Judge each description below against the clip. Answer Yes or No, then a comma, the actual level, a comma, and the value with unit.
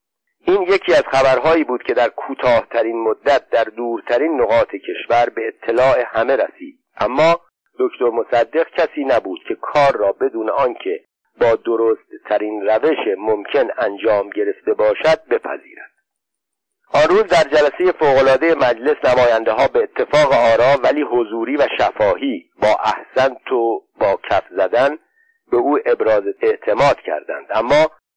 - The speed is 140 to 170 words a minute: No, average, 130 wpm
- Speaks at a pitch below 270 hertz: No, very high, 340 Hz